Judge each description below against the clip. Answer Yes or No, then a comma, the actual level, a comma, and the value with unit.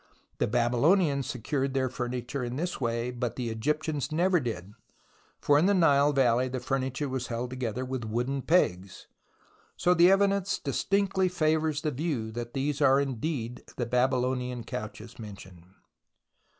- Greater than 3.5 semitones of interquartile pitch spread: Yes, average, 4.1 semitones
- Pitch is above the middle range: No, low, 130 Hz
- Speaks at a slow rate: No, average, 150 wpm